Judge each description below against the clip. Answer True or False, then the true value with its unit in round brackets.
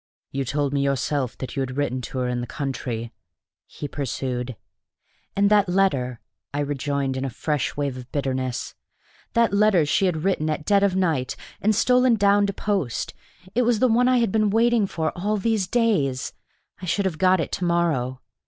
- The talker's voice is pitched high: False (155 Hz)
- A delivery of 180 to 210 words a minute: True (190 wpm)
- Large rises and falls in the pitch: True (7.2 semitones)